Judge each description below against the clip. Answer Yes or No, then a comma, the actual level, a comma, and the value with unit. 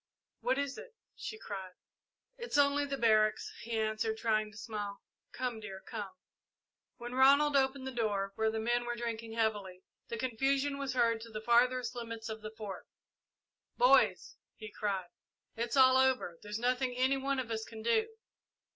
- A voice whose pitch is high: Yes, high, 230 Hz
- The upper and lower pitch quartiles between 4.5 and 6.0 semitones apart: No, average, 3.3 semitones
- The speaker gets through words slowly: No, average, 170 wpm